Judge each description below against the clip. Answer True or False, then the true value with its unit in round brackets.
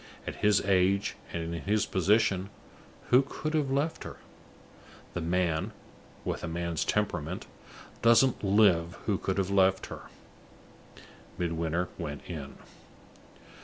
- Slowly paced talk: True (125 wpm)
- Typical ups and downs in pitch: True (3.7 semitones)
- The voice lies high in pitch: False (95 Hz)